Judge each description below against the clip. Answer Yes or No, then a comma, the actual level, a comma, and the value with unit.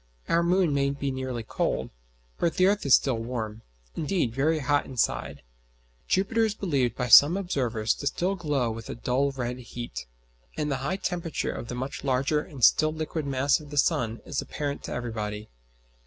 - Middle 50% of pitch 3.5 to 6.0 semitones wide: Yes, average, 4.5 semitones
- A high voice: No, medium, 140 Hz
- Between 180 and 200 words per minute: Yes, average, 185 wpm